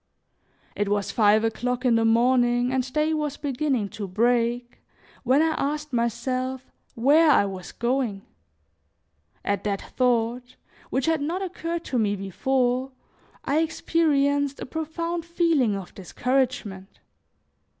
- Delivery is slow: Yes, slow, 130 wpm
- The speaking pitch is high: Yes, very high, 255 Hz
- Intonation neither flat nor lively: Yes, average, 4.5 semitones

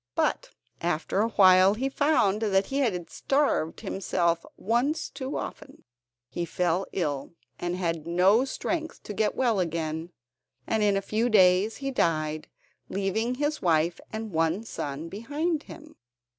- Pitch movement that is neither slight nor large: No, wide, 5.7 semitones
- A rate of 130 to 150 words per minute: Yes, average, 145 wpm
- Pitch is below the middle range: No, high, 195 Hz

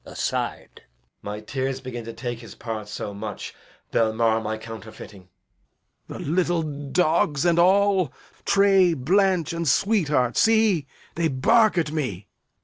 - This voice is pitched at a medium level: Yes, medium, 145 Hz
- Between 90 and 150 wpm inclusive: Yes, average, 145 wpm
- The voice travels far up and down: Yes, wide, 7.9 semitones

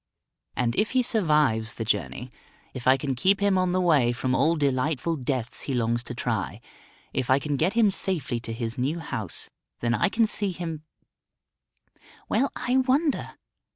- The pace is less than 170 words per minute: No, average, 175 wpm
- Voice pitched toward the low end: No, medium, 150 Hz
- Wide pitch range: Yes, wide, 7.4 semitones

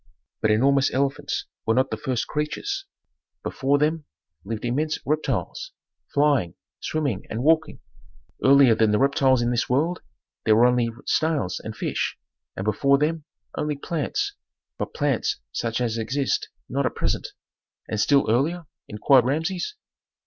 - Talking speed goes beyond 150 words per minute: No, average, 140 wpm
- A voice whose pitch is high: No, medium, 140 Hz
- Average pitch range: Yes, average, 4.6 semitones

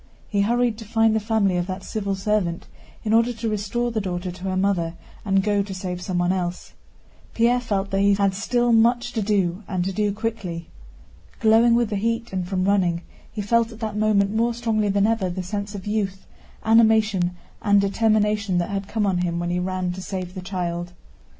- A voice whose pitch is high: Yes, high, 200 Hz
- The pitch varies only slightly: No, average, 3.0 semitones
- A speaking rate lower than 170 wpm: No, fast, 205 wpm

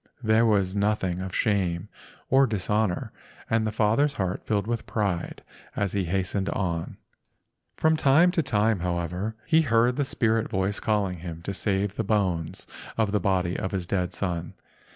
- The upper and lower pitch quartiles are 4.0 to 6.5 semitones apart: No, average, 3.5 semitones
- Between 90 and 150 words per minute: No, average, 160 wpm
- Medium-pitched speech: No, low, 100 Hz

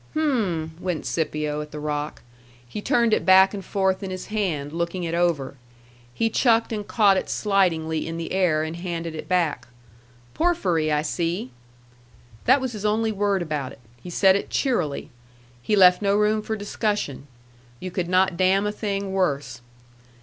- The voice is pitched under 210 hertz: Yes, medium, 185 Hz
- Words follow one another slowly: No, average, 170 wpm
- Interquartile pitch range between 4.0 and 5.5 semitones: Yes, average, 4.6 semitones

